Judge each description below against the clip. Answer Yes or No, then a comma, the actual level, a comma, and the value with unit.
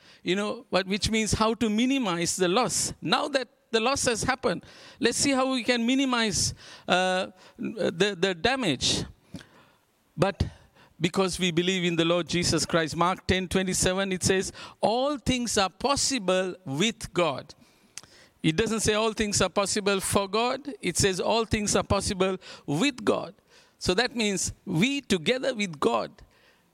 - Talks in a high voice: Yes, high, 205 Hz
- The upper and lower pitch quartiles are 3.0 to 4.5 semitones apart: No, average, 5.1 semitones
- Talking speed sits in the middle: Yes, average, 155 wpm